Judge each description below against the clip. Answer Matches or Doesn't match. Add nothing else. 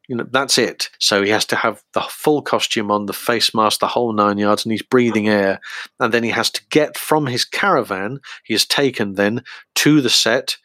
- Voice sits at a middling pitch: Doesn't match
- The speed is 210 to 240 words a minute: Matches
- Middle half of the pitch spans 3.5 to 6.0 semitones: Matches